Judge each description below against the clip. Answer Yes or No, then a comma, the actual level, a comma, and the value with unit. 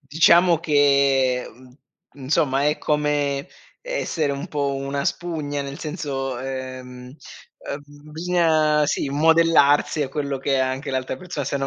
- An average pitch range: No, narrow, 2.2 semitones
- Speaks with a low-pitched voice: No, medium, 145 Hz